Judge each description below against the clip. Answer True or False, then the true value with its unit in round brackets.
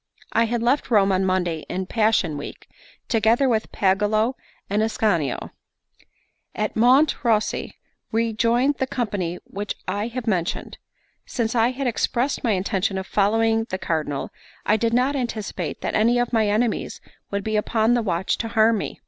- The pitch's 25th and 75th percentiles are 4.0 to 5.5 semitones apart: False (3.2 semitones)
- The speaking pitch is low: False (220 Hz)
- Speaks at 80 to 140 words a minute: False (165 wpm)